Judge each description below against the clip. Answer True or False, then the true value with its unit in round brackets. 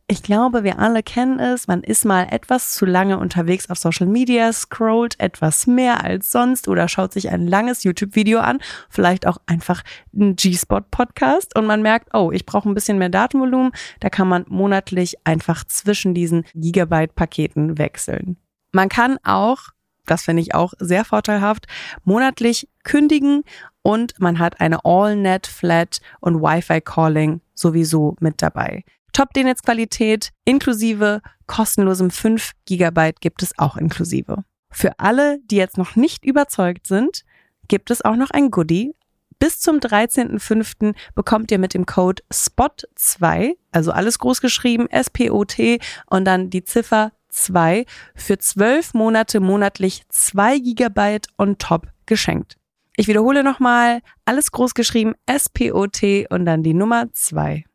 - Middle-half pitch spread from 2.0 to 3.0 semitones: False (5.0 semitones)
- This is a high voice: True (205 Hz)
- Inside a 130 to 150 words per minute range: True (145 wpm)